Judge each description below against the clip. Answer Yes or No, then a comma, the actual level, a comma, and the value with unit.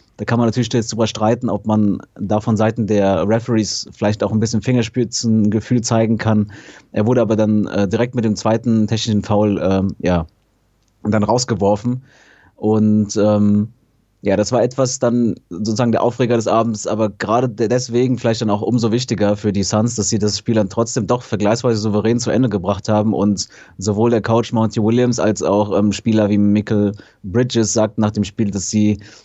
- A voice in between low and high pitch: No, low, 110 Hz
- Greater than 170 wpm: Yes, average, 185 wpm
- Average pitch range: No, narrow, 1.9 semitones